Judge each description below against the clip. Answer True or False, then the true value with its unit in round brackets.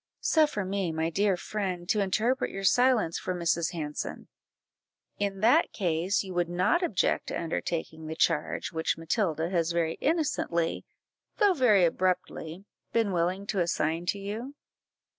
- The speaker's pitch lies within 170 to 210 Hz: True (185 Hz)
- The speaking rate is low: False (145 wpm)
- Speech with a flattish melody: False (3.9 semitones)